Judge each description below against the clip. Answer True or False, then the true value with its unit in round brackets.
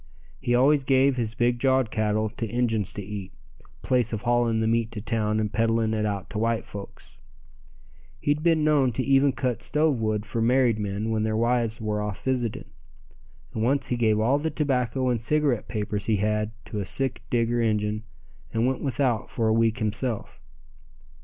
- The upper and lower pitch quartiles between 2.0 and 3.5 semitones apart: True (3.1 semitones)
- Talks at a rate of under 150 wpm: False (185 wpm)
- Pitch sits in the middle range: False (115 Hz)